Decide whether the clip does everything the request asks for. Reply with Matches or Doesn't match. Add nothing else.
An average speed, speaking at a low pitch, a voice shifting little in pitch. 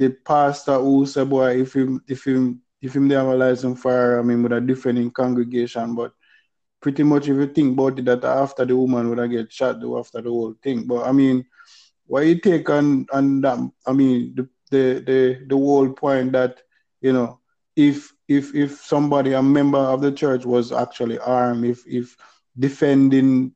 Matches